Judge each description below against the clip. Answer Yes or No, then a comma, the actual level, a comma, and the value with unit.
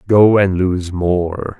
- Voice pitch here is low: Yes, very low, 95 Hz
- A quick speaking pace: No, average, 150 wpm